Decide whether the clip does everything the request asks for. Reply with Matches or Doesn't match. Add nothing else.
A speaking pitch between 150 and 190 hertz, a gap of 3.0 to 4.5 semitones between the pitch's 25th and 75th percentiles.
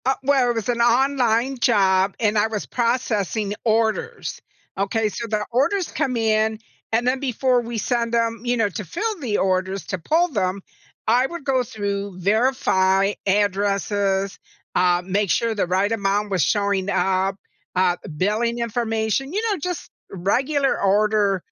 Doesn't match